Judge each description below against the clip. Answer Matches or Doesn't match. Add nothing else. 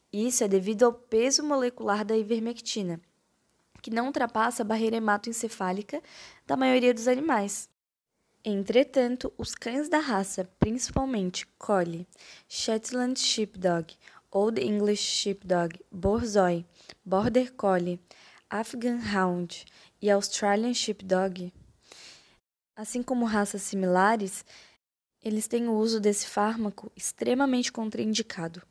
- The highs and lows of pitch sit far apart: Doesn't match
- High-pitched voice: Matches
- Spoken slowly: Matches